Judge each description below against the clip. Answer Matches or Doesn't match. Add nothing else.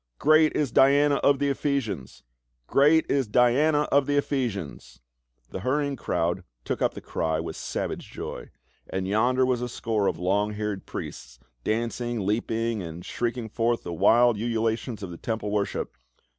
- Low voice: Matches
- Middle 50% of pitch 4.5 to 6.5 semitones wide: Matches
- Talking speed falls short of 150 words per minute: Doesn't match